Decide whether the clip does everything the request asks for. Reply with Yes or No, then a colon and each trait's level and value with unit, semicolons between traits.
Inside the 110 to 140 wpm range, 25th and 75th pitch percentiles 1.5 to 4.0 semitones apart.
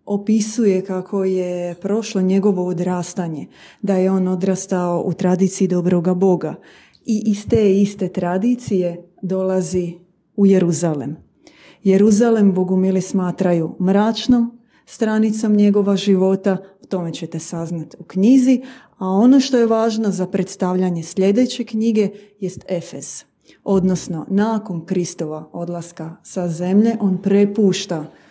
Yes: average, 115 wpm; narrow, 2.5 semitones